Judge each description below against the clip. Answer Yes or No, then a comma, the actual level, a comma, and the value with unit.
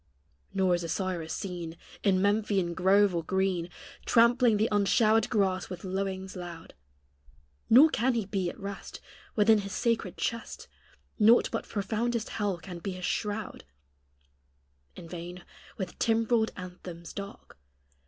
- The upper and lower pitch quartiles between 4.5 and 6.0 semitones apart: No, average, 3.3 semitones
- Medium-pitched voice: No, high, 195 Hz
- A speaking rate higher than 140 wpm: No, slow, 135 wpm